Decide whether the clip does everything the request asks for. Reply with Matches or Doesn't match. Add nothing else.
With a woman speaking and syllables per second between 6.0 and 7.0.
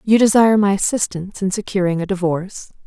Matches